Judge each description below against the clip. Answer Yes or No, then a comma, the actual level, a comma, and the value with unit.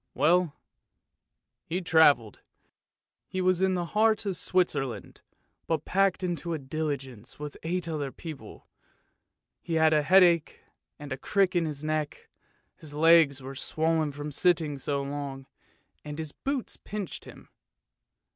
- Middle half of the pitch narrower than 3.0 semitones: No, average, 3.7 semitones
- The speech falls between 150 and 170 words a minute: No, slow, 135 wpm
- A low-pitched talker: No, medium, 160 Hz